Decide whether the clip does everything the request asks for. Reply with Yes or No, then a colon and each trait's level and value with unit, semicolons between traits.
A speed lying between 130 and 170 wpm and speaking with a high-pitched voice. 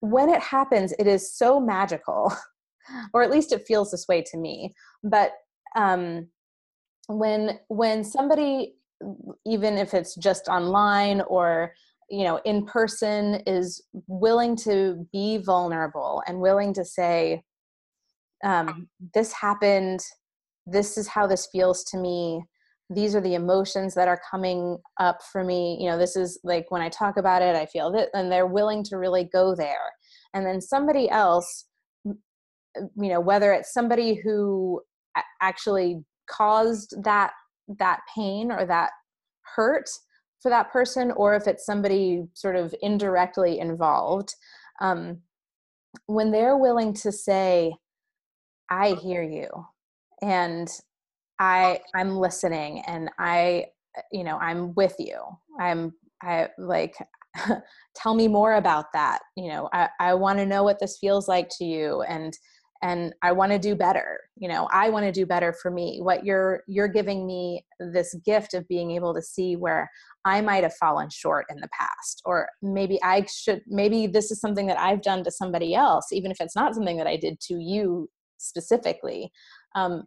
Yes: average, 160 wpm; high, 195 Hz